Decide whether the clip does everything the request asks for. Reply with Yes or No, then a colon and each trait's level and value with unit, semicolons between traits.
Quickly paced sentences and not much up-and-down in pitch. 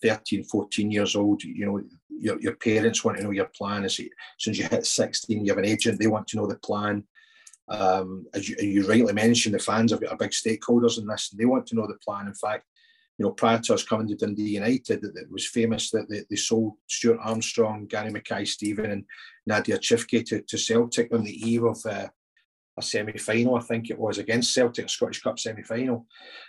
Yes: fast, 220 wpm; narrow, 1.9 semitones